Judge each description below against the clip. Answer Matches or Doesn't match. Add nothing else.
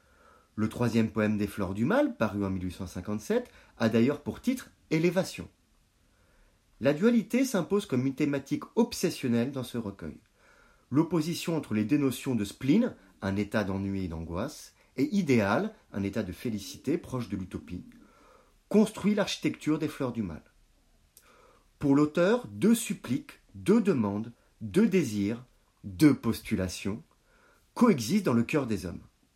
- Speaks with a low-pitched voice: Matches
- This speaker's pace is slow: Matches